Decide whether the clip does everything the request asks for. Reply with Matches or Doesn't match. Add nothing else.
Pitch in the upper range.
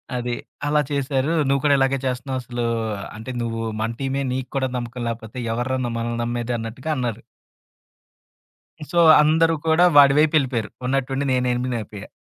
Doesn't match